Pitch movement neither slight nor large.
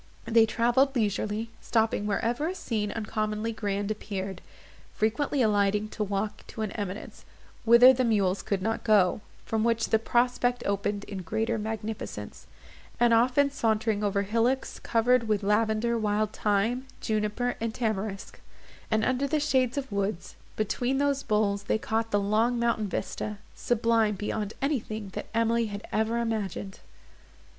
No: narrow, 2.3 semitones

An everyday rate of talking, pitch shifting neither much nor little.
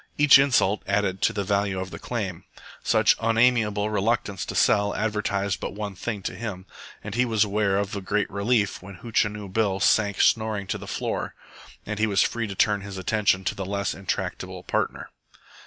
No: average, 190 wpm; narrow, 1.9 semitones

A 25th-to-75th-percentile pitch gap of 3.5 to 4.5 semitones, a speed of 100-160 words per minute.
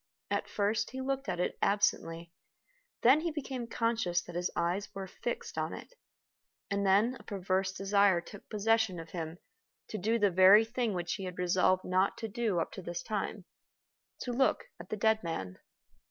No: average, 3.9 semitones; average, 185 wpm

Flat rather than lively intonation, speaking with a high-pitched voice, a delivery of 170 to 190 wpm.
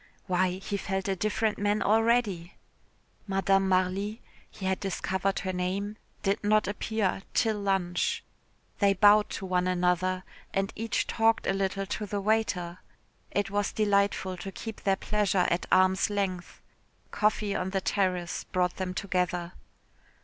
No: narrow, 1.9 semitones; high, 195 Hz; average, 145 wpm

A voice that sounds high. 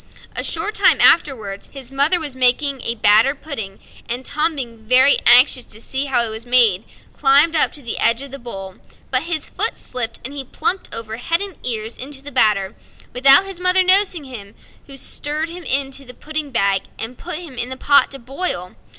Yes: very high, 265 Hz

